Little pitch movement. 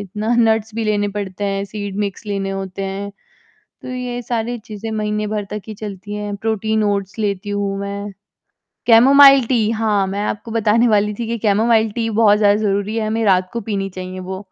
Yes: narrow, 1.9 semitones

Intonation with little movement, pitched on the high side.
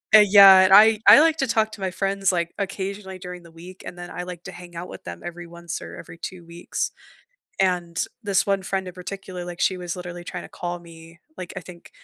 No: narrow, 2.0 semitones; medium, 180 Hz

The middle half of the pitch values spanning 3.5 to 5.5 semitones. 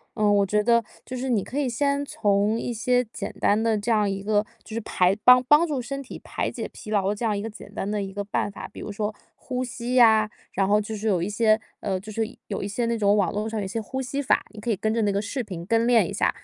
No: average, 2.7 semitones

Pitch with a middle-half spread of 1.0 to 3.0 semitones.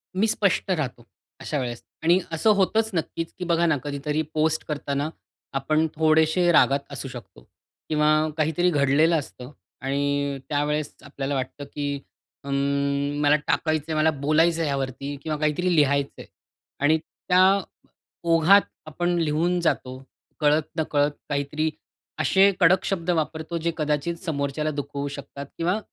Yes: average, 2.7 semitones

